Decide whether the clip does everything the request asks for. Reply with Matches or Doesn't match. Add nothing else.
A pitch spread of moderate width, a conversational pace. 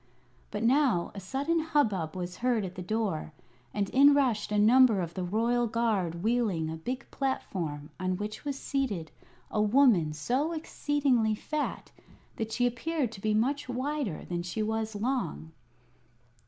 Doesn't match